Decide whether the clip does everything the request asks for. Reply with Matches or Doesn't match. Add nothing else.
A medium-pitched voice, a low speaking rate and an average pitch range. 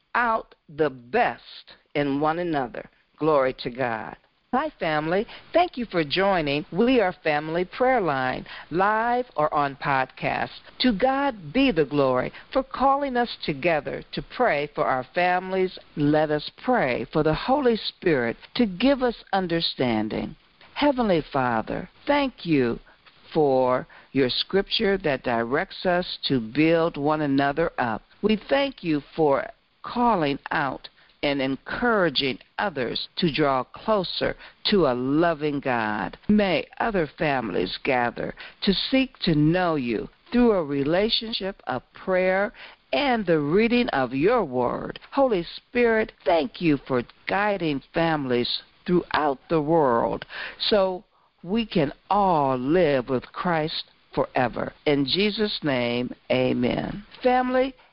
Doesn't match